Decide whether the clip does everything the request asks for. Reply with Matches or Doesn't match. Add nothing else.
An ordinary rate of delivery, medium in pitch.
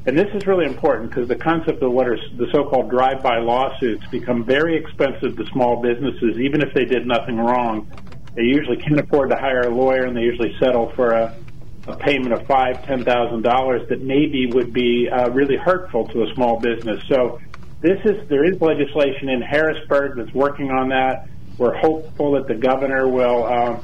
Doesn't match